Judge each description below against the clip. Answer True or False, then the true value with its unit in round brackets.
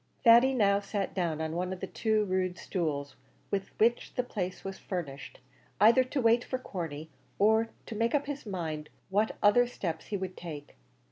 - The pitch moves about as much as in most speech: True (4.9 semitones)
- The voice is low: False (195 Hz)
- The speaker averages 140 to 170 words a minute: False (185 wpm)